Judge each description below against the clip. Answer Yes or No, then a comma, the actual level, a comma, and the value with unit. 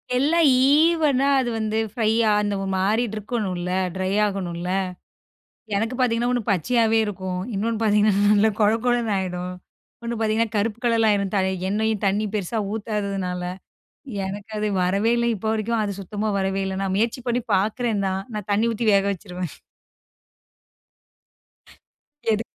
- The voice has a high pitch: Yes, high, 210 Hz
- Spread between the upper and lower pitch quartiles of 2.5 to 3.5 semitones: Yes, average, 2.9 semitones